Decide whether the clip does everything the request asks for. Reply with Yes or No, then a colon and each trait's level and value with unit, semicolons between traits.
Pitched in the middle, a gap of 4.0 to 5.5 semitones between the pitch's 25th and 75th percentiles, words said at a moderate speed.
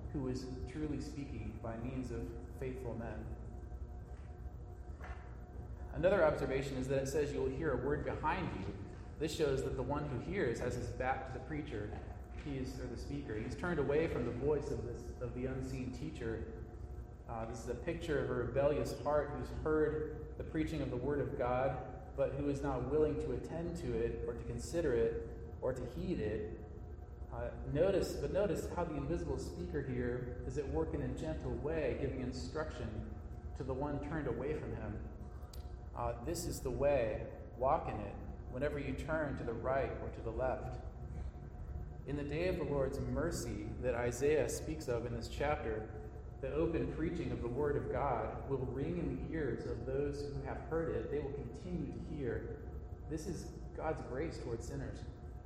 No: low, 125 Hz; average, 4.7 semitones; average, 190 wpm